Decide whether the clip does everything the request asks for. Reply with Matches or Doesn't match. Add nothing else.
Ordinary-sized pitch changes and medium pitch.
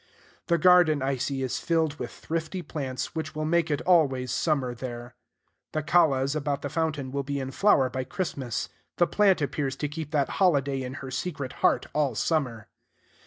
Matches